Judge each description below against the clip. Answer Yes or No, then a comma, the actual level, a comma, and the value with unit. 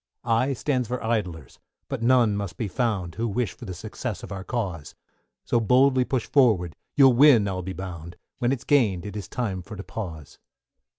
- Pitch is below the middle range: Yes, low, 110 Hz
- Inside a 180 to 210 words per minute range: Yes, average, 190 wpm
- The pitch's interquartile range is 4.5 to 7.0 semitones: Yes, average, 5.0 semitones